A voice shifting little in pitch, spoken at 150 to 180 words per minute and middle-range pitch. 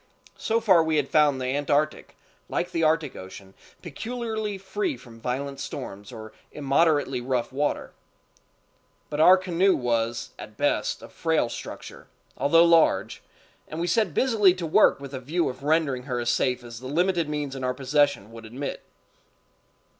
No: average, 5.0 semitones; average, 160 wpm; medium, 145 Hz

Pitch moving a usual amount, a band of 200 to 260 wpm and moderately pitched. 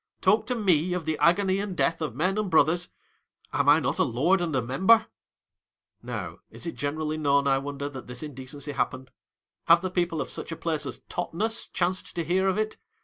Yes: average, 4.5 semitones; fast, 205 wpm; medium, 165 Hz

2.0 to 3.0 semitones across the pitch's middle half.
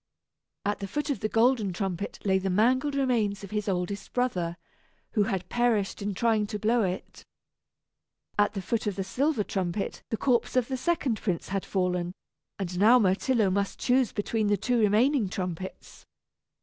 No: average, 3.9 semitones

